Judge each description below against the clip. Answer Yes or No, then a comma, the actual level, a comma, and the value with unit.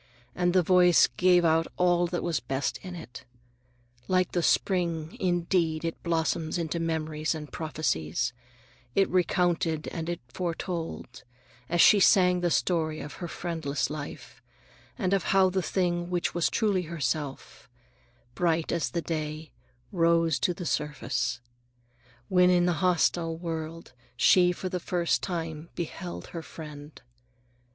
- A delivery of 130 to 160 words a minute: Yes, average, 140 wpm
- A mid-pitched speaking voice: Yes, medium, 170 Hz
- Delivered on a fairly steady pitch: Yes, narrow, 2.1 semitones